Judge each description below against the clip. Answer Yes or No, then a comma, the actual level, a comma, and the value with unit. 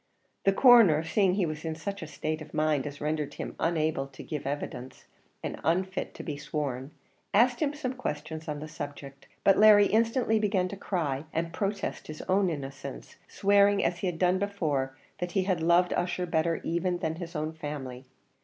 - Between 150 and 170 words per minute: No, average, 190 wpm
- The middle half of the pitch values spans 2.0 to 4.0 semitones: No, average, 4.5 semitones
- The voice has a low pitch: No, medium, 165 Hz